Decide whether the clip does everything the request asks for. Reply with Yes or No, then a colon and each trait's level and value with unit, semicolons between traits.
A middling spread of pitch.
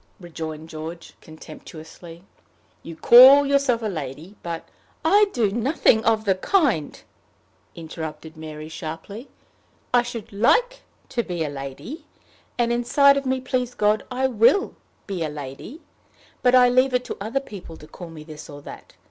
No: wide, 7.9 semitones